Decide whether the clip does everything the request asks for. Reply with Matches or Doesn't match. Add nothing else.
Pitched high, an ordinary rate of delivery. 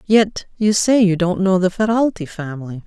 Matches